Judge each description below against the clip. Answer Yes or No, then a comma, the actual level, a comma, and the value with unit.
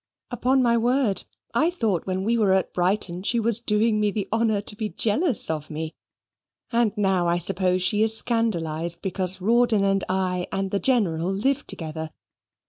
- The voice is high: Yes, high, 200 Hz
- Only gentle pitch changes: No, average, 4.1 semitones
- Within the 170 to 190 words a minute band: Yes, average, 175 wpm